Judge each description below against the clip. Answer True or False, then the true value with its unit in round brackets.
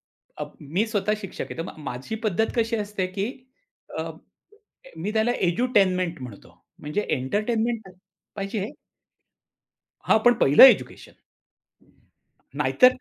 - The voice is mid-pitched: False (205 Hz)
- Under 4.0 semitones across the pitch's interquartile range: False (4.5 semitones)